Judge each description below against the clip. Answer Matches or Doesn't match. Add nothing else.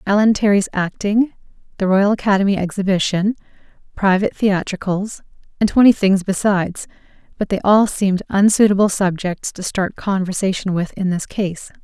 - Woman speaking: Matches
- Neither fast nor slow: Doesn't match